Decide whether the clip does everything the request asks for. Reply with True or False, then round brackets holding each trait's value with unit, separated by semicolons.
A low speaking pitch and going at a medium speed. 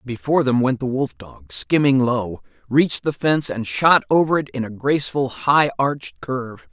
True (130 Hz; 190 wpm)